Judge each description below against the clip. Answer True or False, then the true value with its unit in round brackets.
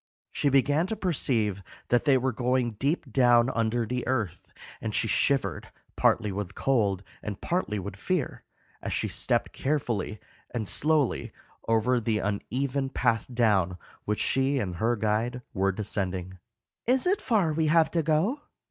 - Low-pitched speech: True (120 Hz)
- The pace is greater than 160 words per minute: False (155 wpm)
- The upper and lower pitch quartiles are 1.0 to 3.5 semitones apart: False (5.1 semitones)